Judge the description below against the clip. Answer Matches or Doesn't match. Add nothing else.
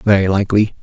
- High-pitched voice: Doesn't match